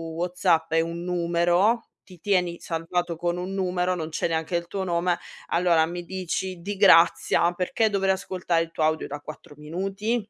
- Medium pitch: Yes, medium, 175 Hz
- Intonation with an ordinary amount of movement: No, narrow, 2.0 semitones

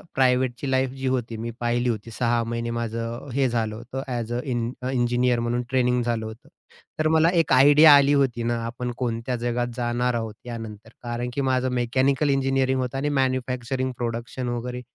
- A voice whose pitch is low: Yes, low, 120 Hz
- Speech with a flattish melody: Yes, narrow, 1.9 semitones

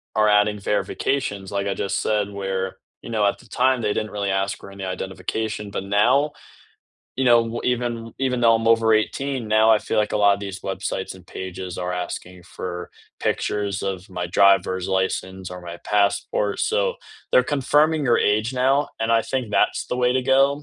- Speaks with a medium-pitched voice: No, low, 105 Hz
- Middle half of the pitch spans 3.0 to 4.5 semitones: Yes, average, 3.9 semitones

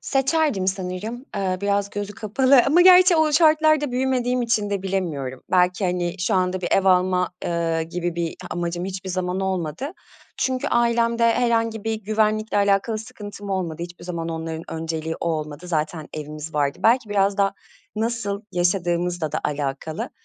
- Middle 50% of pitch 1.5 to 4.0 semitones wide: No, average, 4.7 semitones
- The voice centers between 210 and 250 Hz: No, high, 190 Hz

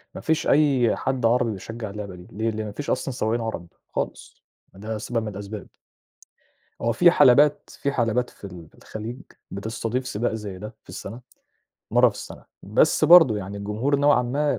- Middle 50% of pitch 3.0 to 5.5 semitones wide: Yes, average, 3.6 semitones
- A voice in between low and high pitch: No, low, 115 Hz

